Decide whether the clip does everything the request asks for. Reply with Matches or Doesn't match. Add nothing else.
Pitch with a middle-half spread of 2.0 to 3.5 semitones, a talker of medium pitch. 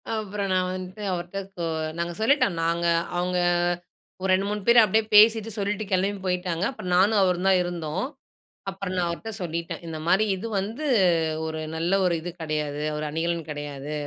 Matches